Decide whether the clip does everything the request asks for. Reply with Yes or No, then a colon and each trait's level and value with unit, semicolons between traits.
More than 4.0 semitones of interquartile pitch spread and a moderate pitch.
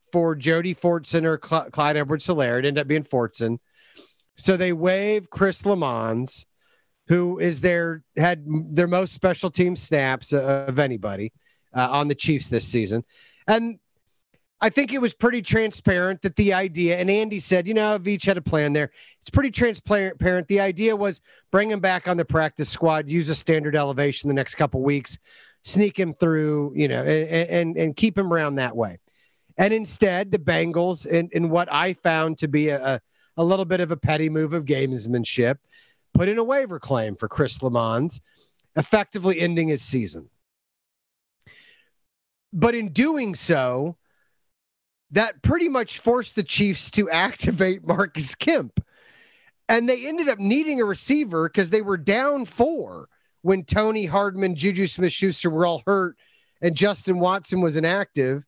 Yes: average, 5.1 semitones; medium, 175 Hz